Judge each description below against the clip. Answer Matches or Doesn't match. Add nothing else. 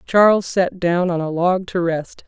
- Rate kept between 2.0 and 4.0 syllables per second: Doesn't match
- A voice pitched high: Doesn't match